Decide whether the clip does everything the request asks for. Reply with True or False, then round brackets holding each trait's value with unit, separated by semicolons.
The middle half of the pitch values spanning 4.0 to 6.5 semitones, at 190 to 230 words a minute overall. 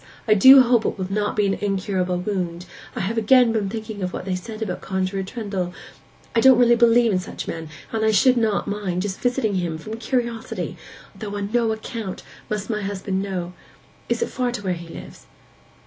False (3.4 semitones; 200 wpm)